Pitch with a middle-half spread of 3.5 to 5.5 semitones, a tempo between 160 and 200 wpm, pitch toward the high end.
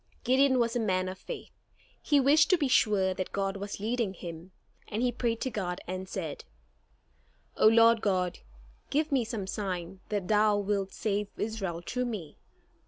Yes: average, 3.9 semitones; average, 170 wpm; high, 210 Hz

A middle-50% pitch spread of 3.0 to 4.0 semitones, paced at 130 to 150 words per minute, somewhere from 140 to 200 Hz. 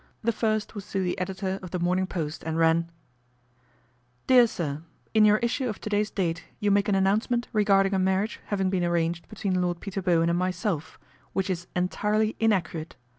No: average, 3.5 semitones; average, 195 wpm; high, 190 Hz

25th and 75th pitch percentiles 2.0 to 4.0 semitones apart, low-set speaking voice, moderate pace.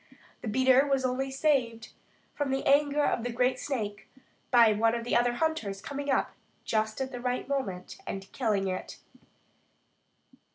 No: average, 3.7 semitones; very high, 250 Hz; average, 160 wpm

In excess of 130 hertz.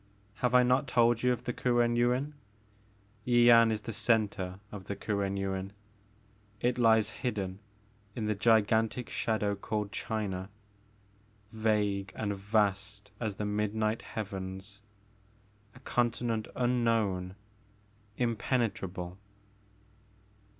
No: low, 110 Hz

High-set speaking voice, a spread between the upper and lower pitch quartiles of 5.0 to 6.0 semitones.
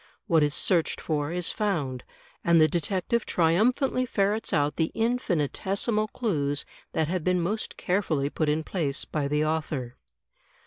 No: medium, 170 Hz; average, 5.3 semitones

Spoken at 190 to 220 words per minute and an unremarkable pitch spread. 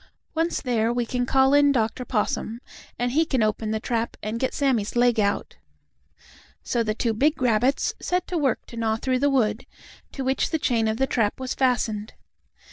Yes: average, 195 wpm; average, 3.4 semitones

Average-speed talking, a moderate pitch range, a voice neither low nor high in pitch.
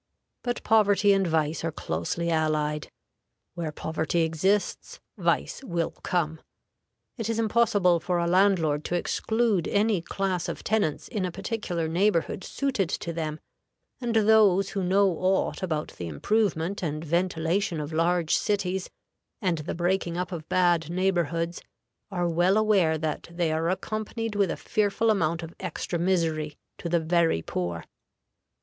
Yes: average, 145 wpm; average, 3.7 semitones; medium, 175 Hz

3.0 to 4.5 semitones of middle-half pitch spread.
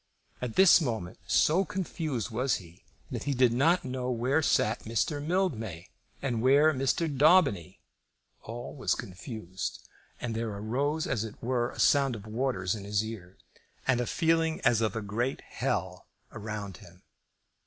No: average, 5.0 semitones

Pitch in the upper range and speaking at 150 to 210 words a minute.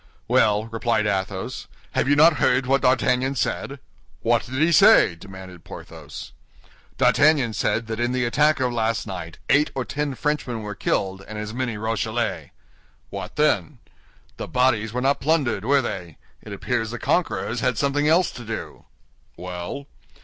No: low, 120 Hz; average, 160 wpm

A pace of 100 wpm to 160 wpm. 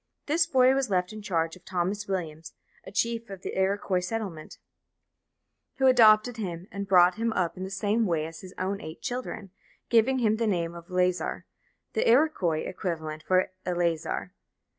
No: average, 170 wpm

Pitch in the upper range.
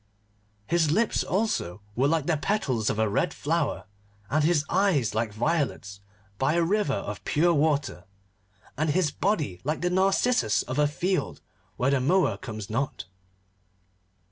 No: medium, 150 Hz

